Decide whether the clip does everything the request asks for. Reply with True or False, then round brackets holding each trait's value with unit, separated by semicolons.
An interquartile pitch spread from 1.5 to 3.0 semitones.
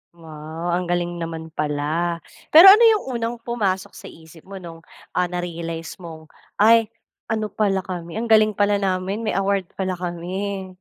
False (3.5 semitones)